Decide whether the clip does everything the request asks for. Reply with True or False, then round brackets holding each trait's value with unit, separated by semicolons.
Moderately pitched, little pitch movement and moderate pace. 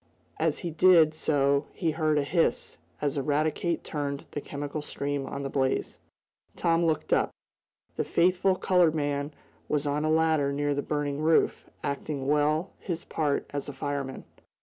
True (150 Hz; 2.1 semitones; 160 wpm)